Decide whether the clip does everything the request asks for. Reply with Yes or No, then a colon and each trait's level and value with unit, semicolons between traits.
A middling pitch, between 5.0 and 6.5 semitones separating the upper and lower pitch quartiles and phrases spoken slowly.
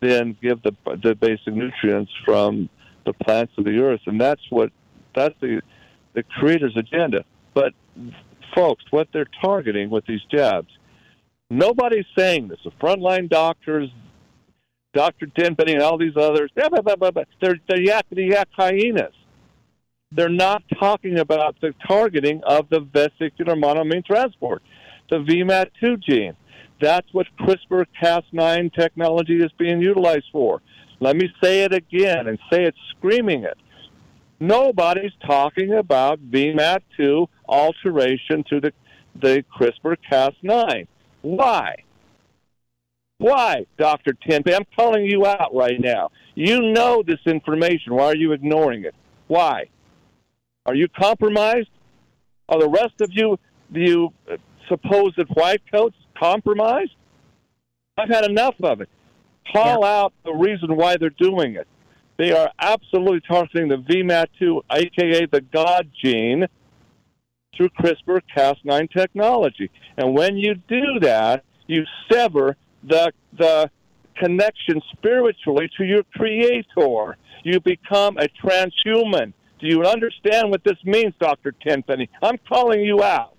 Yes: medium, 170 Hz; average, 5.3 semitones; slow, 130 wpm